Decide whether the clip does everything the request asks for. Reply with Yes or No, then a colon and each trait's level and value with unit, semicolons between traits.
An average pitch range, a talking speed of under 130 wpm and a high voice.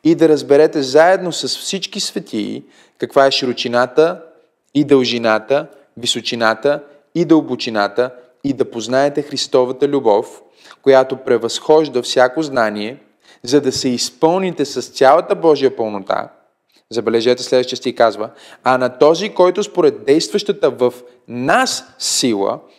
No: average, 4.2 semitones; average, 120 wpm; low, 135 Hz